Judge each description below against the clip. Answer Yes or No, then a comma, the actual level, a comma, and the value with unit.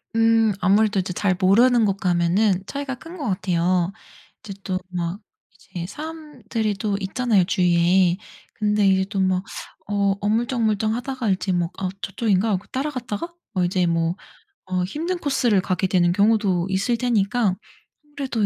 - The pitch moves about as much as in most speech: Yes, average, 3.9 semitones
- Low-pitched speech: No, high, 200 Hz